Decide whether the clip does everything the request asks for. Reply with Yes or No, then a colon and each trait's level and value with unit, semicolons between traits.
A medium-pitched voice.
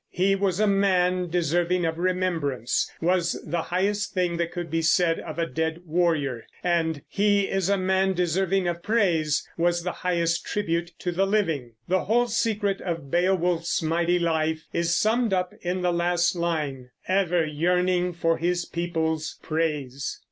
Yes: medium, 175 Hz